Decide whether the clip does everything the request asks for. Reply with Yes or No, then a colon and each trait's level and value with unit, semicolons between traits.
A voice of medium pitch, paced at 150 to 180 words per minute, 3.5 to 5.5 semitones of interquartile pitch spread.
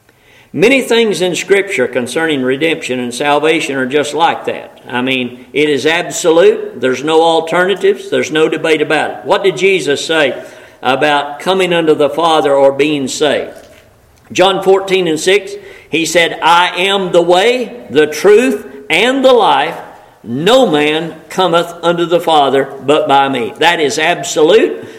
Yes: medium, 165 Hz; average, 155 wpm; average, 4.7 semitones